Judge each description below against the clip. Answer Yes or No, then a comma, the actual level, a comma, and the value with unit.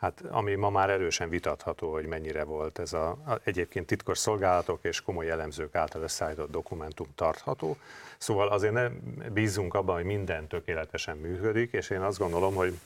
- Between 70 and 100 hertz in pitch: Yes, very low, 95 Hz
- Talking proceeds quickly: Yes, fast, 170 wpm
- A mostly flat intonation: No, average, 4.2 semitones